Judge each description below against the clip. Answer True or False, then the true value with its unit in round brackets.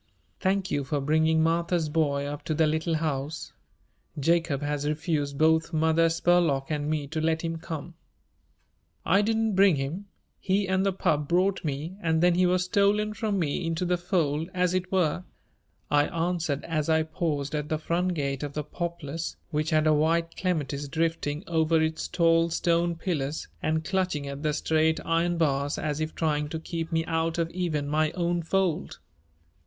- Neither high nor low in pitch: True (160 Hz)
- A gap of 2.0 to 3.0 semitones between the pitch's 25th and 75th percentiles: True (2.5 semitones)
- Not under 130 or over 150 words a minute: False (180 wpm)